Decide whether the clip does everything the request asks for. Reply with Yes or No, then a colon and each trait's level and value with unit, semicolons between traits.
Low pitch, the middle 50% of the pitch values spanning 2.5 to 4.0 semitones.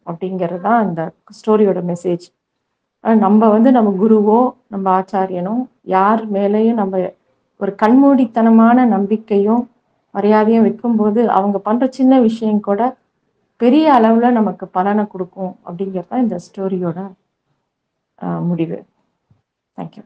No: high, 210 Hz; average, 3.4 semitones